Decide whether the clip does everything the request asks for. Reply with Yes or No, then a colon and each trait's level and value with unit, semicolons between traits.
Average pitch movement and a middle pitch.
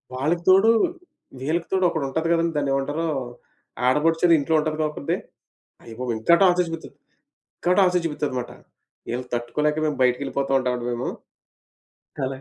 Yes: average, 4.3 semitones; medium, 150 Hz